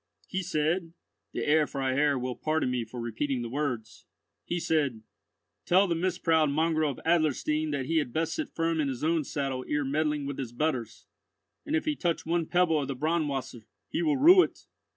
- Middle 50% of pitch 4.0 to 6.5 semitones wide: No, average, 3.6 semitones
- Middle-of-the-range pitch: Yes, medium, 155 Hz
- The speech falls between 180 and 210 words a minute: Yes, average, 185 wpm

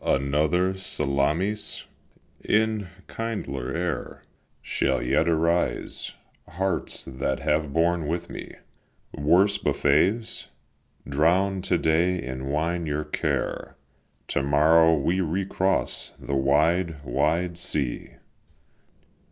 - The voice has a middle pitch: No, very low, 80 Hz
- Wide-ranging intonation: No, average, 4.1 semitones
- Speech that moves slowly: Yes, slow, 95 wpm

